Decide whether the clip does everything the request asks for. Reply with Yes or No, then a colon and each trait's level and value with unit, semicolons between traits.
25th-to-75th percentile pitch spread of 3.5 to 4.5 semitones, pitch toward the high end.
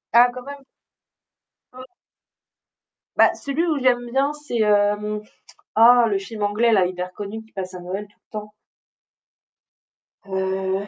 Yes: average, 3.9 semitones; high, 210 Hz